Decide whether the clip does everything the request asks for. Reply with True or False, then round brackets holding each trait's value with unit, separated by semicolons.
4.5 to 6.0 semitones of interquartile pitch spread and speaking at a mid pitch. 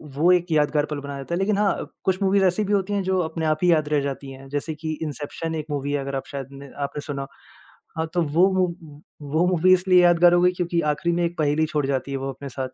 False (3.8 semitones; 160 Hz)